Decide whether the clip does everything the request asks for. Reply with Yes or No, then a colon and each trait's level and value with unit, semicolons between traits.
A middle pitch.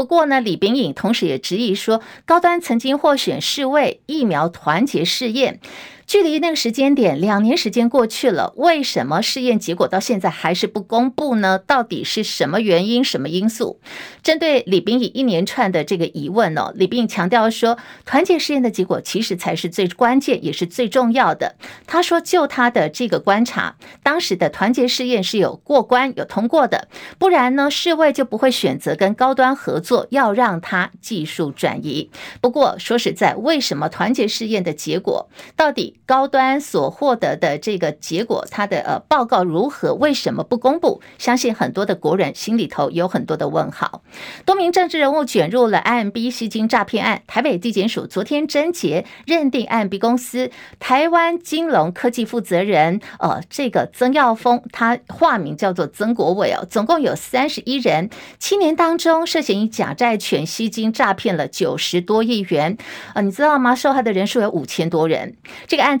No: high, 240 Hz